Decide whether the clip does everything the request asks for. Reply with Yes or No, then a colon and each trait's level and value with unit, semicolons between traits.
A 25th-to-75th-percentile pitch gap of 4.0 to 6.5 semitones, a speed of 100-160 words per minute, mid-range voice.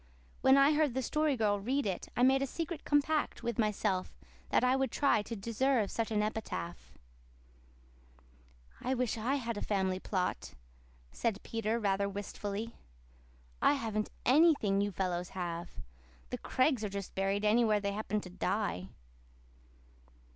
No: average, 4.7 semitones; average, 150 wpm; high, 220 Hz